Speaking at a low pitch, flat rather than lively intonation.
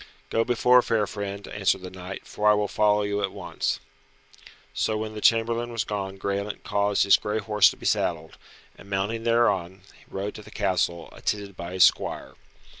Yes: low, 105 Hz; narrow, 2.0 semitones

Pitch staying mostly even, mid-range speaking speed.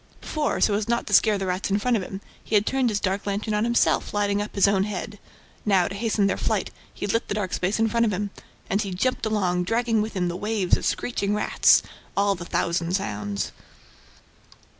No: narrow, 2.3 semitones; fast, 225 wpm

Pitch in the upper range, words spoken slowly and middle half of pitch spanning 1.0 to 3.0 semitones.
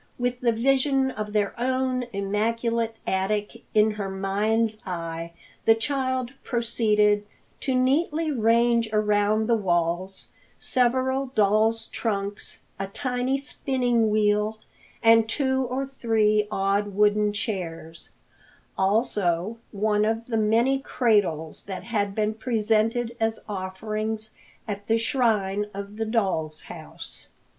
Yes: high, 220 Hz; slow, 115 wpm; average, 2.7 semitones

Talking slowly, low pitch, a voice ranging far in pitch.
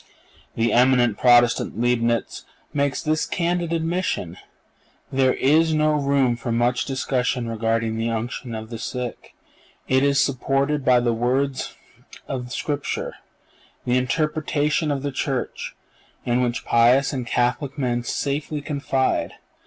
No: slow, 130 wpm; low, 130 Hz; average, 3.0 semitones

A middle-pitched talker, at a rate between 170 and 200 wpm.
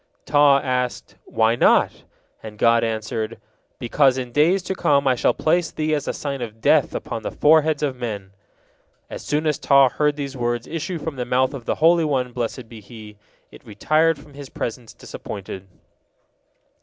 No: low, 130 Hz; average, 180 wpm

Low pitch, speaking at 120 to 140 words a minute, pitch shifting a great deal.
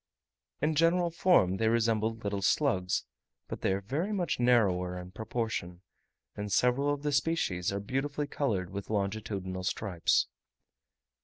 Yes: low, 110 Hz; slow, 135 wpm; wide, 6.9 semitones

